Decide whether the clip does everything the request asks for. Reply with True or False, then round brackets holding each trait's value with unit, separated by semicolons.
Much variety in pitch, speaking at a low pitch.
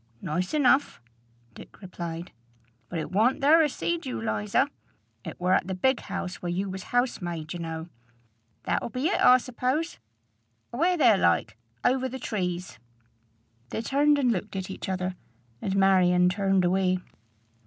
False (6.3 semitones; 195 Hz)